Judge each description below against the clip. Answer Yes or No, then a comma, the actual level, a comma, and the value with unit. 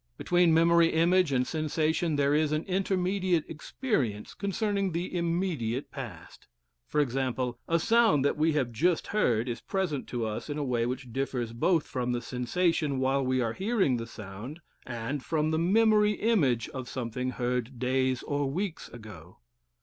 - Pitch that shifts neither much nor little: No, wide, 5.7 semitones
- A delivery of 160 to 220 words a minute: Yes, average, 165 wpm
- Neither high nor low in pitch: Yes, medium, 145 Hz